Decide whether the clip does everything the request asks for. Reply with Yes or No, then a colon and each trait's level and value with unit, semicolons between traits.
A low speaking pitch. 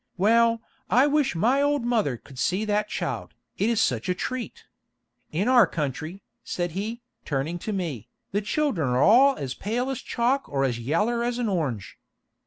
No: high, 210 Hz